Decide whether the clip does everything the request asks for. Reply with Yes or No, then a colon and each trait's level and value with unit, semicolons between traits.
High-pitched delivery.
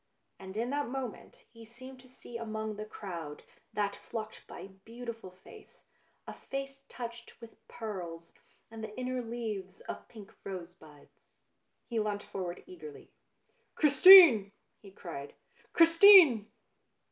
Yes: high, 220 Hz